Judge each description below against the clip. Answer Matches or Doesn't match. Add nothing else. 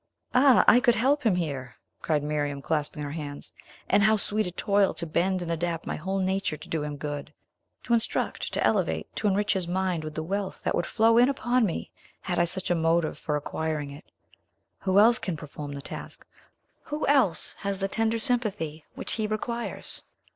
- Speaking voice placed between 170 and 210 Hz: Matches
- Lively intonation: Matches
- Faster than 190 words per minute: Matches